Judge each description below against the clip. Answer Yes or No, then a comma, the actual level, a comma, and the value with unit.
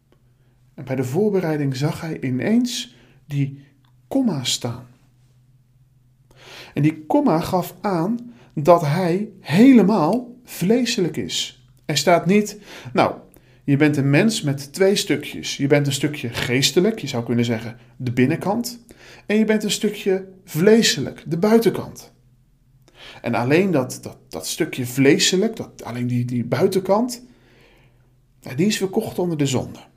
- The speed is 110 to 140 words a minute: Yes, slow, 135 wpm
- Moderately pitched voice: Yes, medium, 145 Hz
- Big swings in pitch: Yes, wide, 7.3 semitones